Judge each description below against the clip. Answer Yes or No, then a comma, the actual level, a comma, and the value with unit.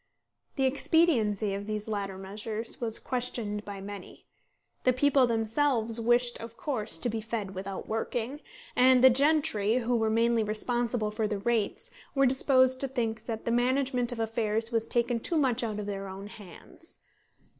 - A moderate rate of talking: Yes, average, 165 wpm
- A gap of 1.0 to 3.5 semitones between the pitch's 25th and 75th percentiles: Yes, average, 3.1 semitones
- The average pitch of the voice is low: No, high, 230 Hz